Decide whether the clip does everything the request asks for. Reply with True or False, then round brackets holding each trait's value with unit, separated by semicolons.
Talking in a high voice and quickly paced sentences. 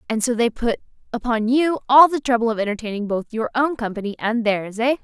True (235 Hz; 215 wpm)